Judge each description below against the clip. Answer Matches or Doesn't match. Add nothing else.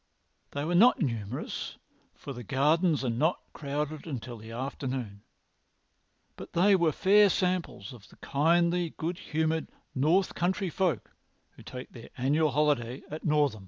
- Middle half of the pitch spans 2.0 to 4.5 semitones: Doesn't match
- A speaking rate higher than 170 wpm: Doesn't match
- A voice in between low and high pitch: Matches